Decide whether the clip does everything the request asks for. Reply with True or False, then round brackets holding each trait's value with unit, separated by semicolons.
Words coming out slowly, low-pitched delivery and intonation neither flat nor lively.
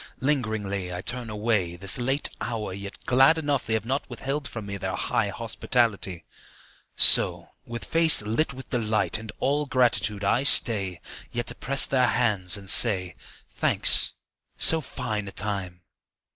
False (155 wpm; 110 Hz; 4.6 semitones)